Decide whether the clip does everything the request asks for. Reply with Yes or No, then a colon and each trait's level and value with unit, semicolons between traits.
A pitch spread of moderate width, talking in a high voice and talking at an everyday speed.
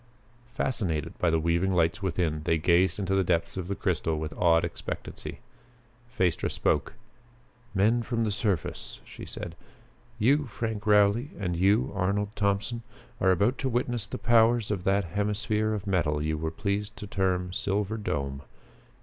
No: average, 4.0 semitones; low, 100 Hz; average, 160 wpm